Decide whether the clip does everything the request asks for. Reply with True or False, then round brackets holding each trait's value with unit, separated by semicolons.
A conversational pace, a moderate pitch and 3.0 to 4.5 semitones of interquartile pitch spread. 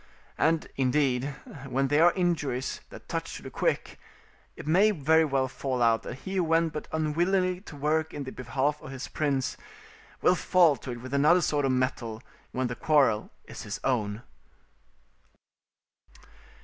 True (160 wpm; 145 Hz; 3.9 semitones)